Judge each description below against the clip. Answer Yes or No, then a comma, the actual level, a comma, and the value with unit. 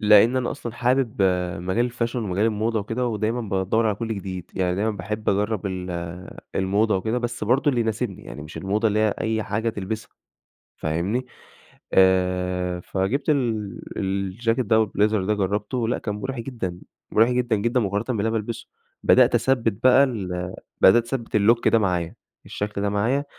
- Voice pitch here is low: Yes, low, 110 Hz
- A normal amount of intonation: Yes, average, 3.4 semitones